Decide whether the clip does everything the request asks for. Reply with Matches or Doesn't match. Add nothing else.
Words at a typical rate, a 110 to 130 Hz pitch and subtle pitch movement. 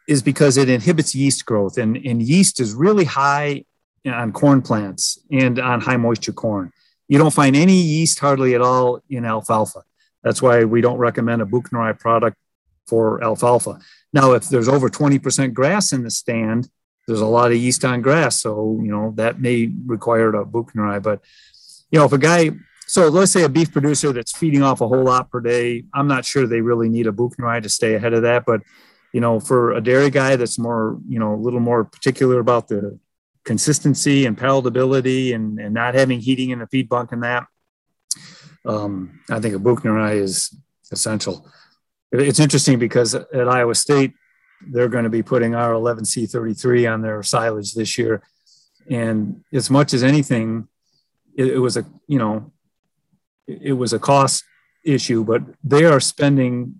Doesn't match